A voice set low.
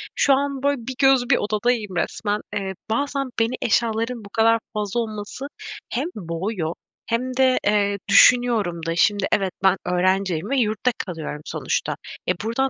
No: high, 220 Hz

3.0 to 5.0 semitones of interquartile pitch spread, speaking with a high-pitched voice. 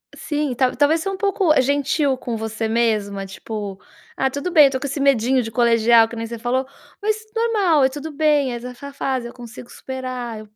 Yes: average, 4.0 semitones; very high, 260 Hz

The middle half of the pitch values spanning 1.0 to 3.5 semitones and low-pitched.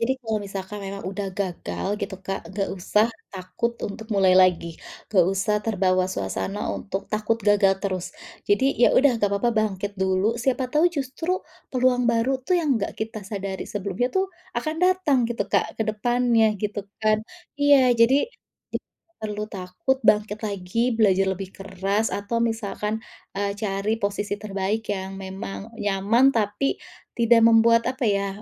No: average, 3.0 semitones; high, 210 Hz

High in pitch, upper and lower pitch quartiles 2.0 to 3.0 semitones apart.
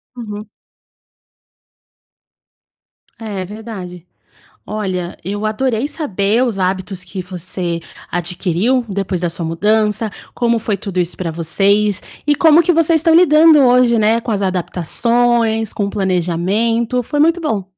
No: high, 210 Hz; average, 4.5 semitones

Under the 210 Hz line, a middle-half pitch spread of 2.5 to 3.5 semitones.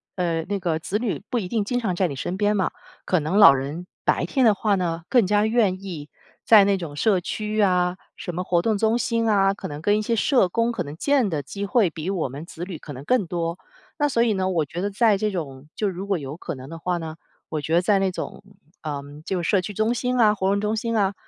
No: high, 190 Hz; average, 4.2 semitones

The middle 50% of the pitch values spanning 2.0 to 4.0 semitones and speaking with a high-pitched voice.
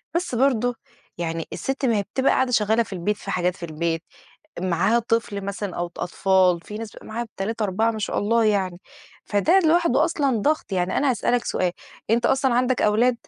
No: average, 4.6 semitones; high, 220 Hz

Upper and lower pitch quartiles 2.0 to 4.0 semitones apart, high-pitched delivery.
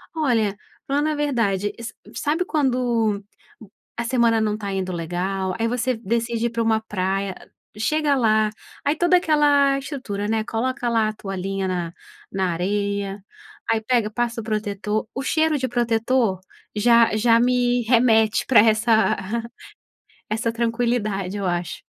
Yes: average, 3.4 semitones; high, 225 Hz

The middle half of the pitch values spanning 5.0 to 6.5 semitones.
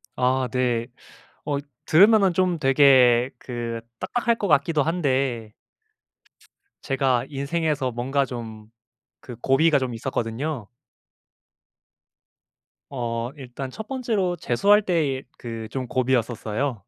No: average, 4.5 semitones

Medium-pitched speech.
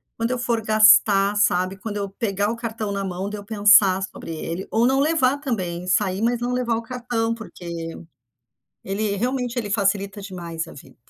No: high, 210 Hz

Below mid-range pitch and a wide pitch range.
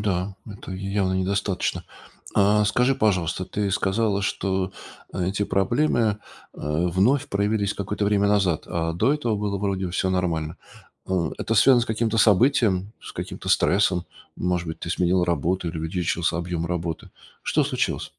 No: very low, 95 Hz; average, 2.8 semitones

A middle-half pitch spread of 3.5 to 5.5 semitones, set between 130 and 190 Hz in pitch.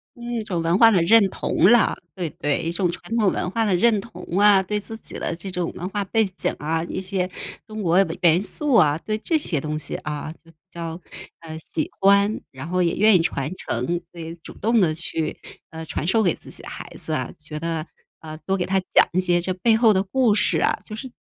Yes: average, 4.3 semitones; medium, 185 Hz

